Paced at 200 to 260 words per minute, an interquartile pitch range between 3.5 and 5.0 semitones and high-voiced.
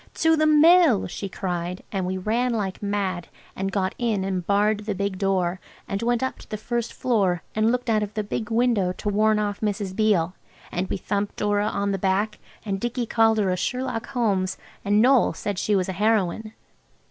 No: fast, 205 wpm; average, 2.9 semitones; high, 205 Hz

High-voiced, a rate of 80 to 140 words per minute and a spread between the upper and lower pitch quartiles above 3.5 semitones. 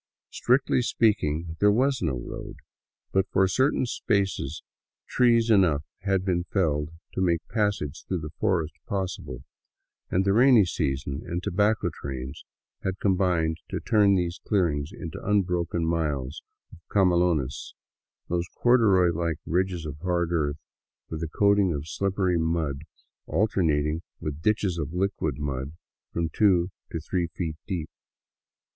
No: very low, 85 Hz; slow, 135 wpm; average, 4.0 semitones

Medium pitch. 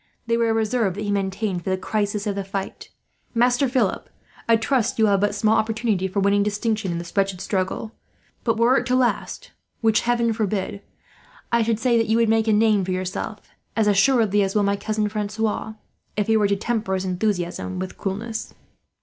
No: high, 210 Hz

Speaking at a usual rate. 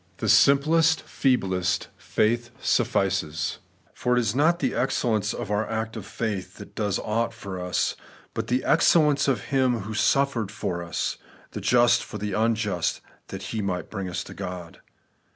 Yes: average, 170 wpm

